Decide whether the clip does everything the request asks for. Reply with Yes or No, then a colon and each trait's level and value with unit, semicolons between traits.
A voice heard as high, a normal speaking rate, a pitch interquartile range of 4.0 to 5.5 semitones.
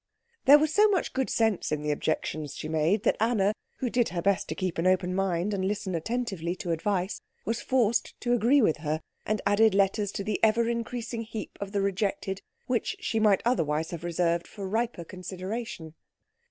Yes: high, 200 Hz; average, 195 wpm; average, 4.6 semitones